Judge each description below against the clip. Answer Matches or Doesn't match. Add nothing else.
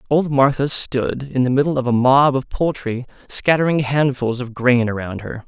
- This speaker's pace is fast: Doesn't match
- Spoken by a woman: Doesn't match